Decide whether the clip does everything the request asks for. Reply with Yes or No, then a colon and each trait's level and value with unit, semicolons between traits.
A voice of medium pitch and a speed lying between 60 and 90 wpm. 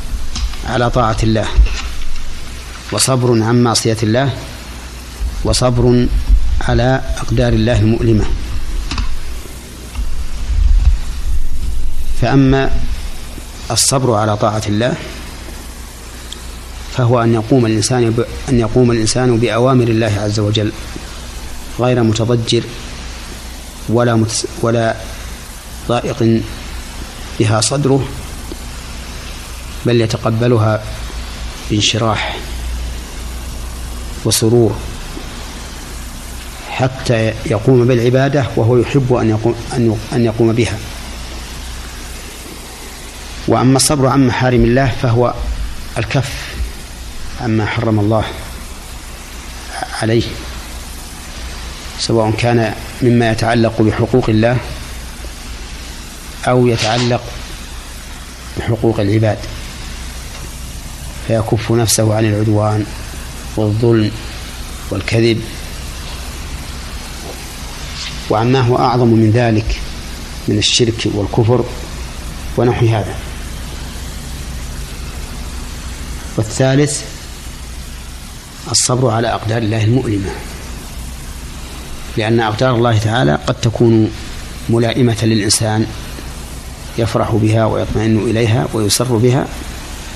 No: very low, 85 Hz; average, 70 wpm